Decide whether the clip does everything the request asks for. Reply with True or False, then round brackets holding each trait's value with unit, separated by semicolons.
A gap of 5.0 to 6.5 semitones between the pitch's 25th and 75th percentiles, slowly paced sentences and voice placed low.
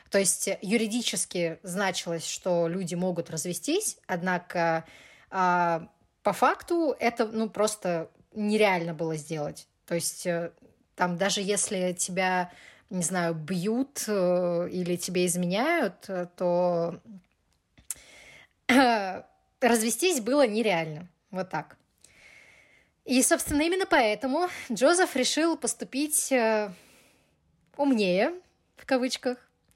False (5.4 semitones; 100 wpm; 195 Hz)